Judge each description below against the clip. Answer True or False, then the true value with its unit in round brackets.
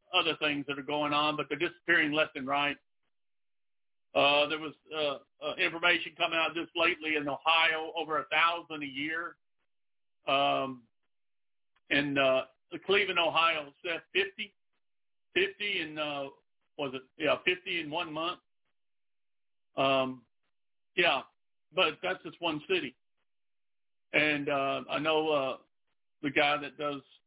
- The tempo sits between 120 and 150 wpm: True (135 wpm)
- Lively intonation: False (2.8 semitones)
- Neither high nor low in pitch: True (150 Hz)